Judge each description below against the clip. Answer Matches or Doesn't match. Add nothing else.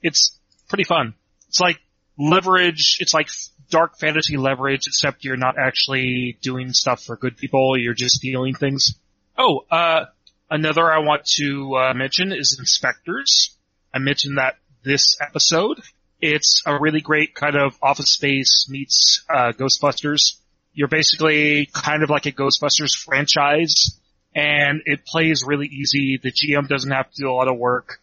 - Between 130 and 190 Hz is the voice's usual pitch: Matches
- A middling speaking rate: Matches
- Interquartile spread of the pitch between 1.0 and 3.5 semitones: Matches